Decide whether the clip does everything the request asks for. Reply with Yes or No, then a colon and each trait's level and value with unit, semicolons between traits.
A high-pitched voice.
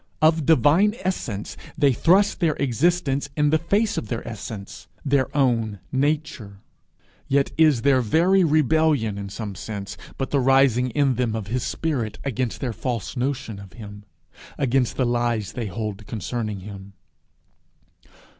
No: low, 125 Hz